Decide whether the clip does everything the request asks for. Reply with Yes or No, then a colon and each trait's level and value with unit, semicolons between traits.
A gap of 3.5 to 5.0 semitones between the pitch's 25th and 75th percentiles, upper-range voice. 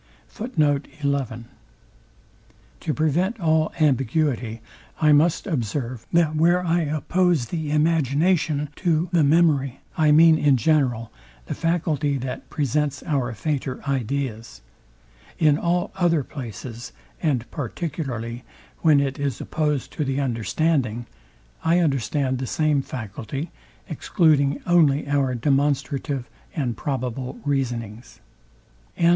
No: average, 3.8 semitones; medium, 145 Hz